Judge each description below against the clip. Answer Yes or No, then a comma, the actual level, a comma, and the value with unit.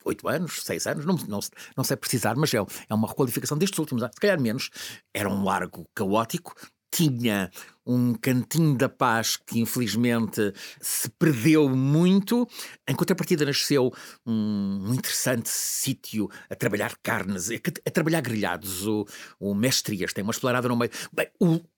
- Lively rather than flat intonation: Yes, wide, 6.2 semitones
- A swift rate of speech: No, average, 150 wpm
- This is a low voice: Yes, low, 125 Hz